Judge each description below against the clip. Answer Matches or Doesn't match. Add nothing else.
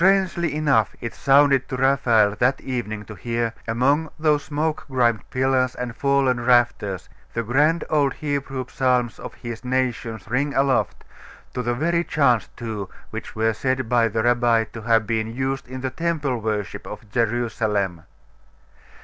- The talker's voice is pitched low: Matches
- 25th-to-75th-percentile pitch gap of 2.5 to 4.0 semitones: Matches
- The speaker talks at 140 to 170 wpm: Matches